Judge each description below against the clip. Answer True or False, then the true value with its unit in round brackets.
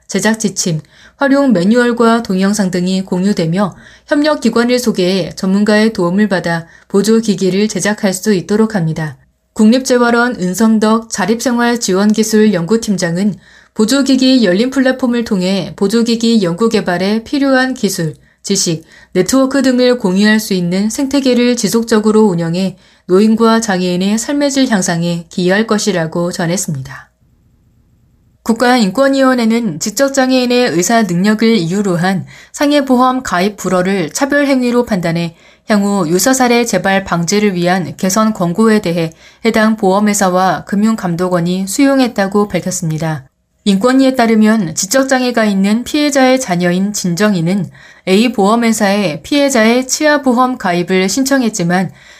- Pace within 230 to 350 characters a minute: True (320 characters per minute)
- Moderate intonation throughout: True (4.6 semitones)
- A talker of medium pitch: False (210 Hz)